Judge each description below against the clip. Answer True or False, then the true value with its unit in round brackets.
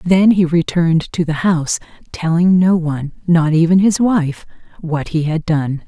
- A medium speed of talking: True (175 wpm)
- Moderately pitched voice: True (170 Hz)